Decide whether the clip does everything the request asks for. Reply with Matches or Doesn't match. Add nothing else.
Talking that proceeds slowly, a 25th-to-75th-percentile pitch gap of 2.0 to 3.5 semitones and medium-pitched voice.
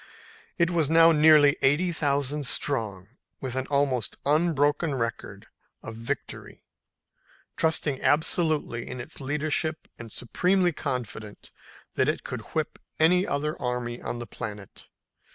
Doesn't match